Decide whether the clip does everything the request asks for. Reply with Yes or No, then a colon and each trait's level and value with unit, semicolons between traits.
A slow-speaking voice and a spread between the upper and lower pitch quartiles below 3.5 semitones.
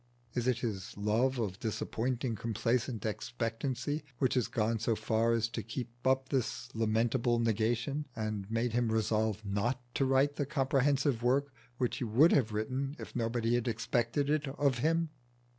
No: average, 160 wpm; average, 3.0 semitones